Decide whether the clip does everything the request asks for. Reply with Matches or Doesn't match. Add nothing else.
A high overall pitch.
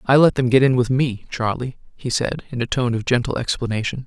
Doesn't match